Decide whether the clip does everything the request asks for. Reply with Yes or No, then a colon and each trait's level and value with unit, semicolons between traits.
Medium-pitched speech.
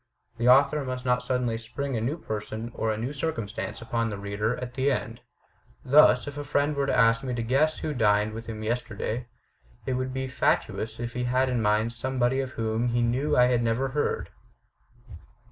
No: low, 125 Hz